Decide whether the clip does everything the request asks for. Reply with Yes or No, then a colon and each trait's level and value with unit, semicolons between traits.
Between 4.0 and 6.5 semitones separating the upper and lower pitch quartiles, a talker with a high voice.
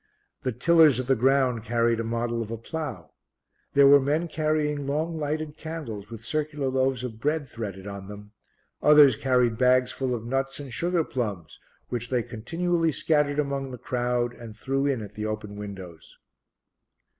No: average, 4.5 semitones; low, 130 Hz